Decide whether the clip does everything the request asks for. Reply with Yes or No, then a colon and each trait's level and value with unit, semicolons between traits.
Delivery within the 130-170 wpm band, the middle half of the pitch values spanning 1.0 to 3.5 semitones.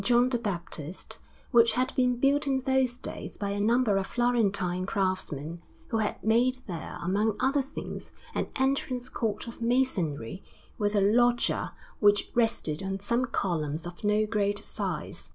No: average, 155 wpm; average, 4.3 semitones